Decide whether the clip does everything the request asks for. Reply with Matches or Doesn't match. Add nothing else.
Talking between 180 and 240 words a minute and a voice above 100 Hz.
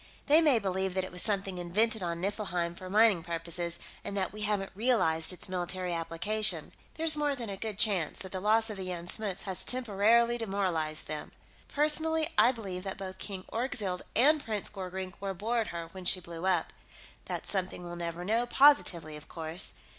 Matches